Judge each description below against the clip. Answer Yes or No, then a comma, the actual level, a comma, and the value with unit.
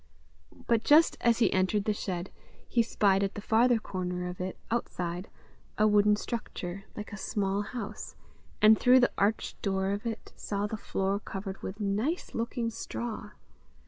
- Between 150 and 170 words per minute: Yes, average, 165 wpm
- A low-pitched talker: No, high, 210 Hz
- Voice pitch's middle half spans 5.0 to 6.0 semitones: No, average, 2.8 semitones